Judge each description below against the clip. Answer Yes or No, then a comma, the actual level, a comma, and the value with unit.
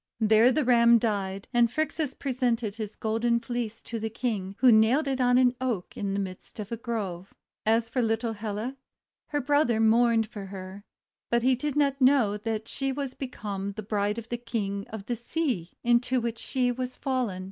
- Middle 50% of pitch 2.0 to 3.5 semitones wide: Yes, average, 3.0 semitones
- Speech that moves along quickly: No, average, 190 wpm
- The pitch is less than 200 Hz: No, high, 230 Hz